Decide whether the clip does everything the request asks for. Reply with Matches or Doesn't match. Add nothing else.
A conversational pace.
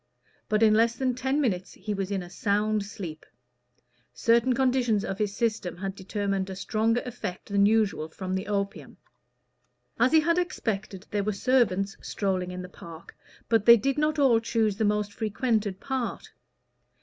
Matches